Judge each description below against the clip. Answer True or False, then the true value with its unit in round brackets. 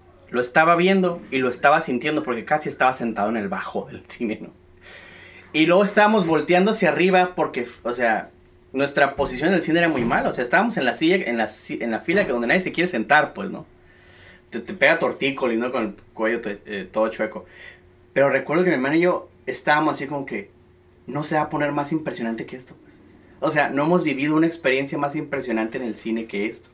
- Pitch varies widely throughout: True (5.7 semitones)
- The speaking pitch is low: False (145 Hz)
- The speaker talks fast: True (225 wpm)